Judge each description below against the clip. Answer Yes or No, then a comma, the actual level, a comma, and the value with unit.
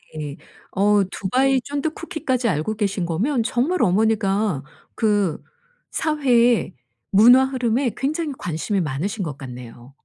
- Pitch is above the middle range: Yes, high, 215 Hz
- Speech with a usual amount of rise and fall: No, wide, 6.7 semitones